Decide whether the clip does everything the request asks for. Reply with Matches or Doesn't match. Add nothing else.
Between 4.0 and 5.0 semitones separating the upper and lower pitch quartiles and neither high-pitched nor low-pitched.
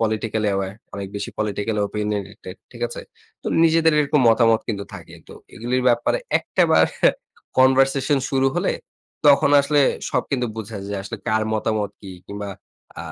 Doesn't match